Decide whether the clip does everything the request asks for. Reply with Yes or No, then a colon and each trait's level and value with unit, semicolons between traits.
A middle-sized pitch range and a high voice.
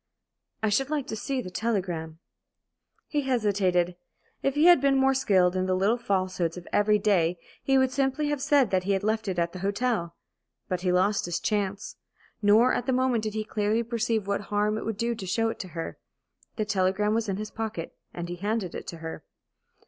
Yes: average, 4.1 semitones; high, 210 Hz